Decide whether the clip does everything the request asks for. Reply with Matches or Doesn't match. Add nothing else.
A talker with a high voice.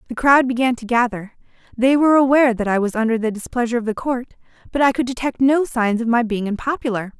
Matches